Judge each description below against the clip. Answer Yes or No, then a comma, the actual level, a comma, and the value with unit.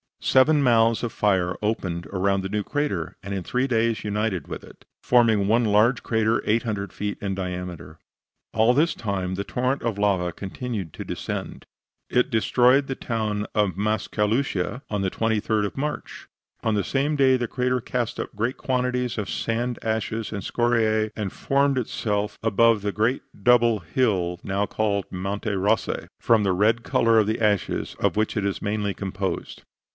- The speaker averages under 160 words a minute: No, average, 170 wpm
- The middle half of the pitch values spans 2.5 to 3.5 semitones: Yes, average, 3.1 semitones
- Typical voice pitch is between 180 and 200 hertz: No, low, 110 Hz